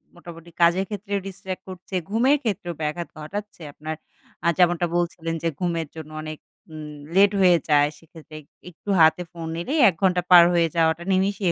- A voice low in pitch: No, medium, 175 Hz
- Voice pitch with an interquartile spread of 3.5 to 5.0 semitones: No, average, 2.7 semitones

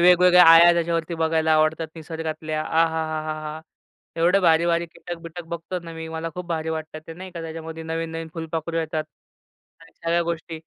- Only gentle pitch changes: Yes, narrow, 1.1 semitones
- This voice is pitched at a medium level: Yes, medium, 165 Hz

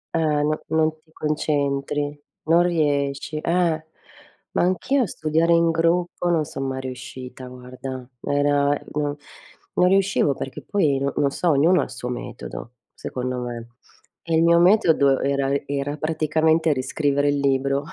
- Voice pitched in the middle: Yes, medium, 145 Hz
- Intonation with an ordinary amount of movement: Yes, average, 3.1 semitones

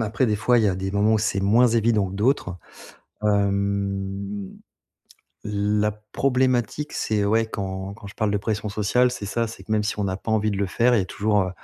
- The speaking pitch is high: No, low, 105 Hz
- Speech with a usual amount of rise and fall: No, narrow, 2.0 semitones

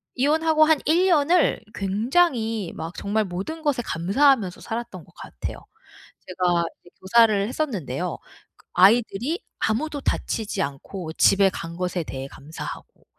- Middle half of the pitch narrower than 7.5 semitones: No, wide, 8.0 semitones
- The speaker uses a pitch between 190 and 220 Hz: Yes, high, 215 Hz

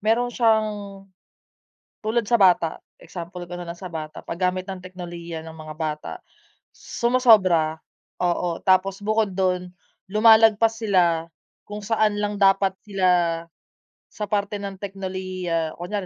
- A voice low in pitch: No, high, 190 Hz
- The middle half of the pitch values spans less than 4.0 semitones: Yes, average, 3.4 semitones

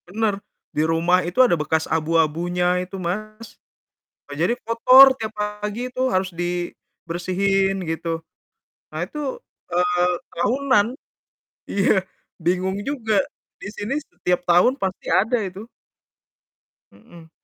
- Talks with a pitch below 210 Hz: Yes, medium, 185 Hz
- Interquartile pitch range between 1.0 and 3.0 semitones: No, average, 3.6 semitones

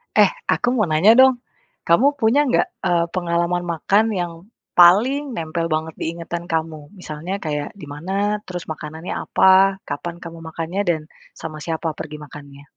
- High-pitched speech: No, medium, 170 Hz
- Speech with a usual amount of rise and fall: Yes, average, 3.6 semitones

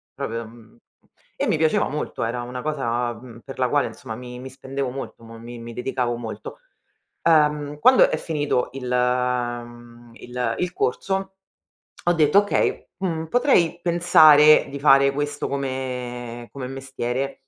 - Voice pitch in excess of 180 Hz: No, low, 130 Hz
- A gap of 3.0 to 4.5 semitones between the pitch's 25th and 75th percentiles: Yes, average, 3.6 semitones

